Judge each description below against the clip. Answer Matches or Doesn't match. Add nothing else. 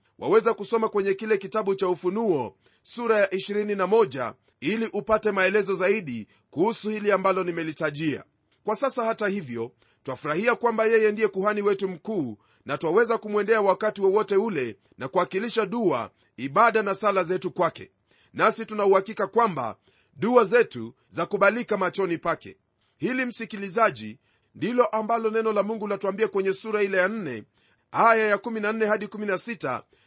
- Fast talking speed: Doesn't match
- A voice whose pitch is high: Matches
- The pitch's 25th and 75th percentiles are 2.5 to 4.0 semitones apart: Matches